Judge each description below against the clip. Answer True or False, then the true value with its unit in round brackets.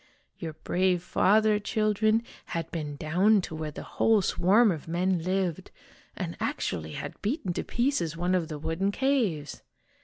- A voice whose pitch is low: False (185 Hz)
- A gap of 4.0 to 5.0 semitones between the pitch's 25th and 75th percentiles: True (4.7 semitones)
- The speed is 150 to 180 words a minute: True (160 wpm)